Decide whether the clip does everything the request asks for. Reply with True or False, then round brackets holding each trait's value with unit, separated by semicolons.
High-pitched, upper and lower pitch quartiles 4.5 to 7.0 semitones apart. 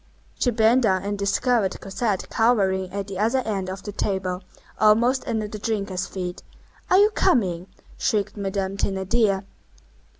False (200 Hz; 2.8 semitones)